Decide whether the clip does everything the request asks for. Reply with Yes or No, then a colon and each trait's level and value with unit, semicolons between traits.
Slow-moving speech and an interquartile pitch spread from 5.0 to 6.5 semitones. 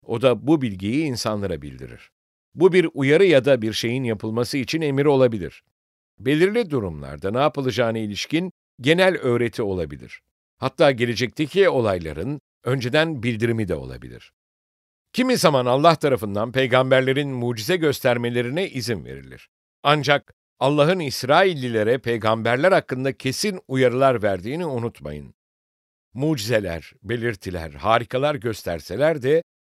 Yes: slow, 110 wpm; average, 5.3 semitones